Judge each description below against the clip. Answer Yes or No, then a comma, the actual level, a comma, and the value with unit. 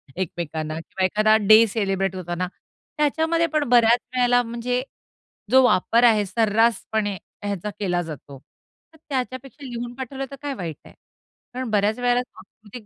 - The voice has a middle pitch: No, high, 225 Hz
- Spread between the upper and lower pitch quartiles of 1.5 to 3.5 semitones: No, average, 4.3 semitones